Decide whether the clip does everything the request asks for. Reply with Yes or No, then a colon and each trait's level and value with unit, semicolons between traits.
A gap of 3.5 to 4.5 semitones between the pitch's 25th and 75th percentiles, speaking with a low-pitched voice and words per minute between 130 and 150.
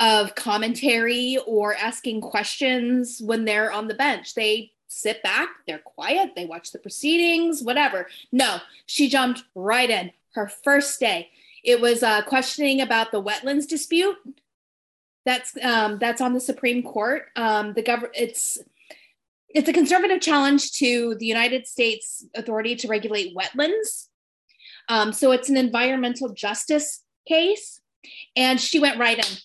No: average, 4.0 semitones; high, 245 Hz; average, 145 wpm